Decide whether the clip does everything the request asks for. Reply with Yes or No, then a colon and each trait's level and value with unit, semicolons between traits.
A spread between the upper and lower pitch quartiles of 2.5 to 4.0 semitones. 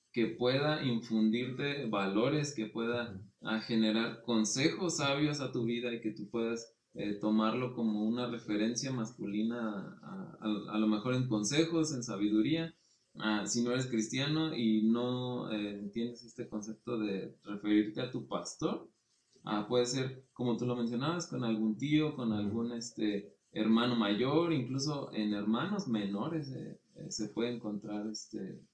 Yes: average, 2.8 semitones